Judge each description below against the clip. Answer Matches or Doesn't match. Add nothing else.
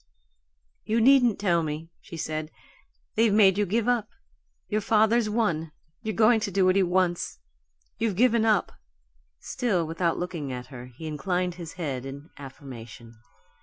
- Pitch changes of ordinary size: Doesn't match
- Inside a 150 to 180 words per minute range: Matches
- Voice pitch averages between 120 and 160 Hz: Doesn't match